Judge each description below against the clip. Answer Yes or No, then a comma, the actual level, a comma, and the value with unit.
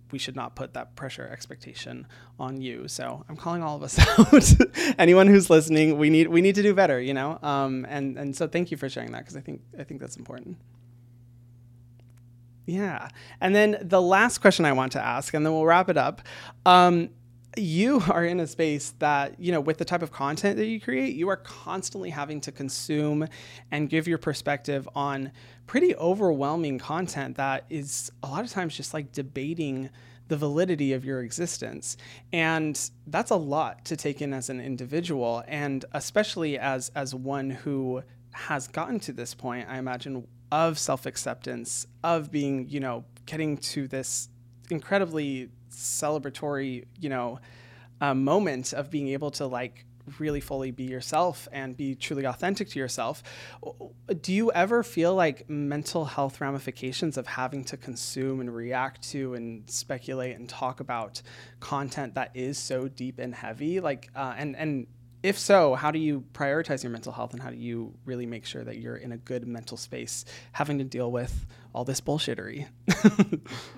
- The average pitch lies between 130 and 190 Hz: Yes, medium, 140 Hz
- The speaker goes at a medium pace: Yes, average, 180 wpm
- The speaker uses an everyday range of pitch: Yes, average, 4.3 semitones